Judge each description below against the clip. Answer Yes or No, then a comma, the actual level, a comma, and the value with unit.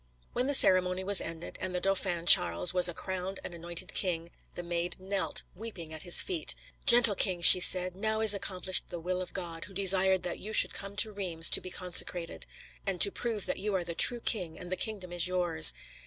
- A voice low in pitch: No, medium, 185 Hz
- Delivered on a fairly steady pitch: Yes, narrow, 2.2 semitones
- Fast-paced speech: Yes, fast, 215 wpm